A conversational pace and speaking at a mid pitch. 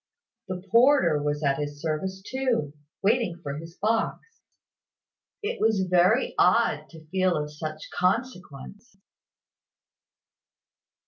No: slow, 110 wpm; medium, 180 Hz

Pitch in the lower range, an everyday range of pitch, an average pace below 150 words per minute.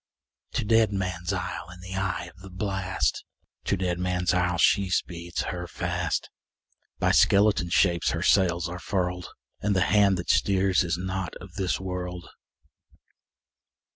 No: very low, 90 Hz; narrow, 1.6 semitones; average, 140 wpm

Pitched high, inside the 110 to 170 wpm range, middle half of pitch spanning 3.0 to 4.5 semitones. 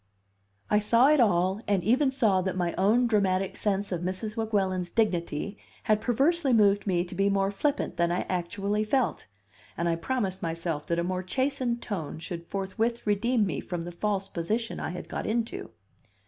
No: high, 200 Hz; average, 180 wpm; average, 4.1 semitones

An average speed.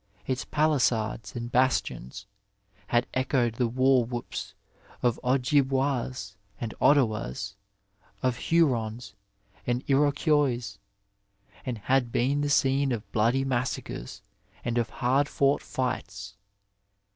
No: slow, 105 wpm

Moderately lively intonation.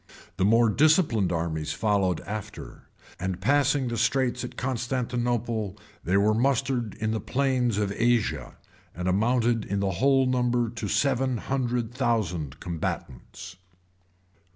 Yes: average, 4.2 semitones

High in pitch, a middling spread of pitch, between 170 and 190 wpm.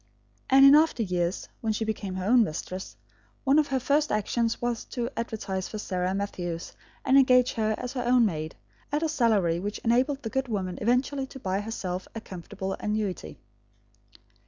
Yes: high, 220 Hz; average, 5.0 semitones; average, 180 wpm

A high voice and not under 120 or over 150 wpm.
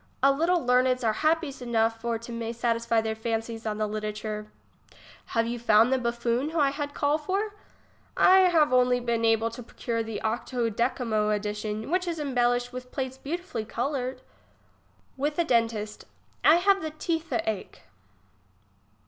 No: high, 240 Hz; average, 165 wpm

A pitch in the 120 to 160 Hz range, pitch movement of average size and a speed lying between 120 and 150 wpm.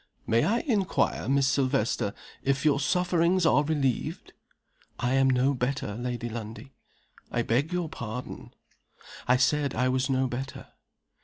Yes: low, 135 Hz; average, 3.0 semitones; average, 140 wpm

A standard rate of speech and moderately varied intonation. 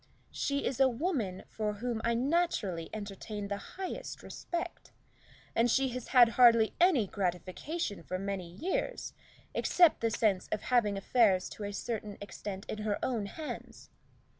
Yes: average, 150 wpm; average, 4.8 semitones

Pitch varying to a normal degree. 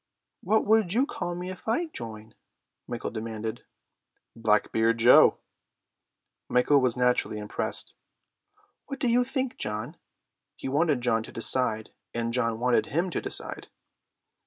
No: wide, 8.2 semitones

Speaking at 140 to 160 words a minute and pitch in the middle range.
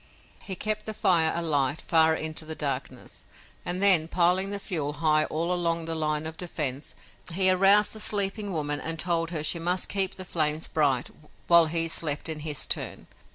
No: average, 185 wpm; medium, 165 Hz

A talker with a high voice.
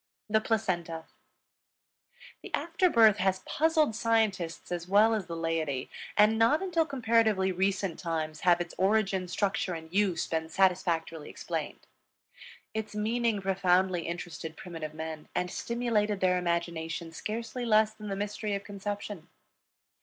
Yes: high, 195 Hz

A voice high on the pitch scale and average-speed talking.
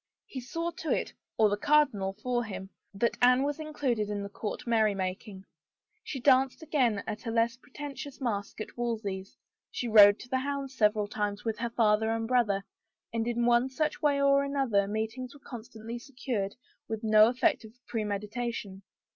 Yes: high, 230 Hz; average, 175 wpm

